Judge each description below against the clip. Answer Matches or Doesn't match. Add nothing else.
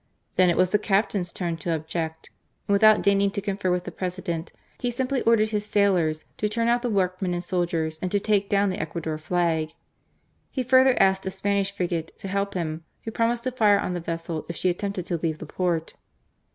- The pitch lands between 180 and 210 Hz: Matches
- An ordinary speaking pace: Doesn't match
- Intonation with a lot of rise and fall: Doesn't match